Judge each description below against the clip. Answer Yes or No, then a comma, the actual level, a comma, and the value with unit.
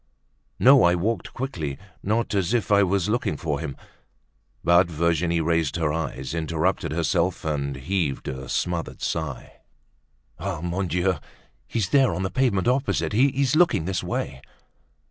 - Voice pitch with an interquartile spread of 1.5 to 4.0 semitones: No, average, 4.4 semitones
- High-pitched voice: No, very low, 85 Hz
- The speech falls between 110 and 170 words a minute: Yes, average, 145 wpm